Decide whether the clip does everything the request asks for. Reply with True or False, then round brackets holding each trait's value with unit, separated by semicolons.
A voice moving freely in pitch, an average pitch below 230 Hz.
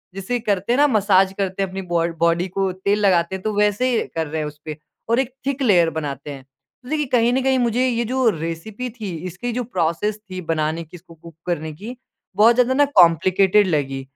True (6.0 semitones; 190 Hz)